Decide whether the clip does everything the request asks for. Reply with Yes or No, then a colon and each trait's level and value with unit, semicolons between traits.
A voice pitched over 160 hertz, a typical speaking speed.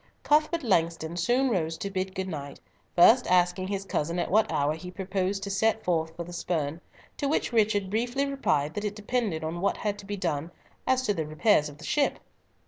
No: high, 190 Hz; fast, 210 wpm